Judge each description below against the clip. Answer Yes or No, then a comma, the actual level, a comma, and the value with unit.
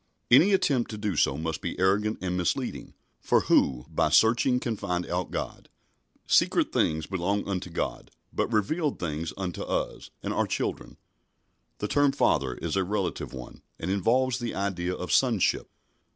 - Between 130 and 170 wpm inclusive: Yes, average, 165 wpm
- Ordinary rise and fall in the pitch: Yes, average, 4.9 semitones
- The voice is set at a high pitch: No, very low, 95 Hz